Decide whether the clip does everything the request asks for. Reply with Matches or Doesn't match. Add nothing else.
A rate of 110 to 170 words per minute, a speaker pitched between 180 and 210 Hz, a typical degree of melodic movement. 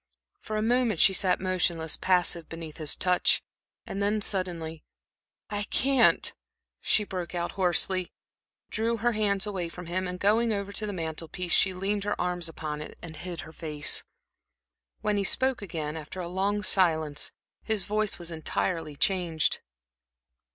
Matches